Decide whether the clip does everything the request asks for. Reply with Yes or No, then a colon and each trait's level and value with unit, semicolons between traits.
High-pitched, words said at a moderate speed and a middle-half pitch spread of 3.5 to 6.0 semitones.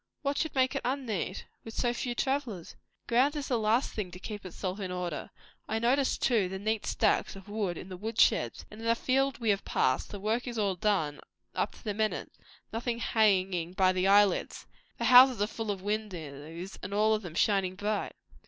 No: high, 210 Hz; fast, 210 wpm; average, 4.0 semitones